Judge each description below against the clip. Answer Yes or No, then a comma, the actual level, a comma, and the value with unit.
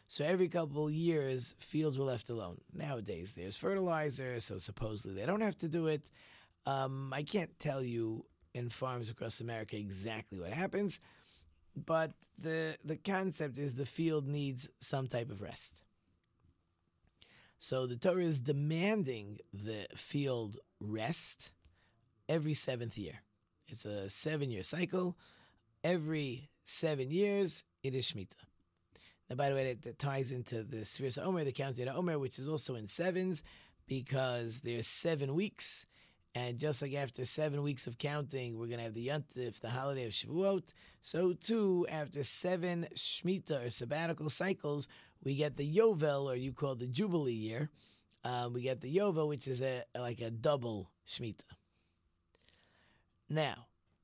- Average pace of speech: Yes, average, 155 wpm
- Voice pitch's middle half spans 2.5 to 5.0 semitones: No, wide, 5.5 semitones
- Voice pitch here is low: Yes, low, 130 Hz